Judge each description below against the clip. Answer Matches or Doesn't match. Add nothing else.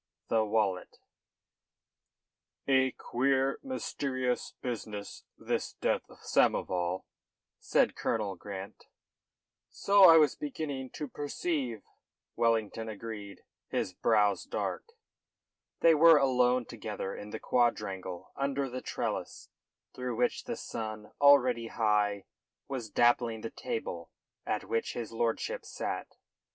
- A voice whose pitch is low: Matches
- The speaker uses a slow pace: Matches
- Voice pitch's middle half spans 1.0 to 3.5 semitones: Doesn't match